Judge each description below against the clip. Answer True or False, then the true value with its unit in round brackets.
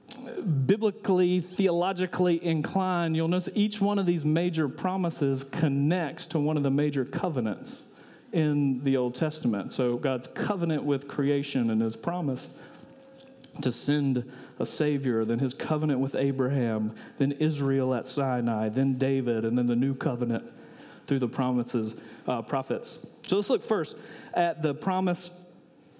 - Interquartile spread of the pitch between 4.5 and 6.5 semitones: True (5.1 semitones)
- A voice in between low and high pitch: True (145 Hz)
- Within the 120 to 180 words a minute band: True (145 wpm)